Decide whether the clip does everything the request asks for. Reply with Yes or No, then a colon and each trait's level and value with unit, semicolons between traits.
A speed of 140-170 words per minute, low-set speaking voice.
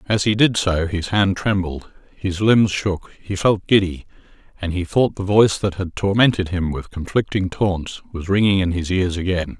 No: average, 195 wpm; very low, 95 Hz